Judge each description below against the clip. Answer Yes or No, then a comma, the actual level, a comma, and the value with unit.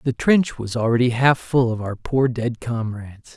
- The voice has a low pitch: Yes, low, 120 Hz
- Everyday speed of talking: Yes, average, 195 wpm